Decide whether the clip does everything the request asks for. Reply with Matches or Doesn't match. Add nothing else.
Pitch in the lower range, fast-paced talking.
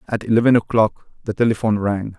Doesn't match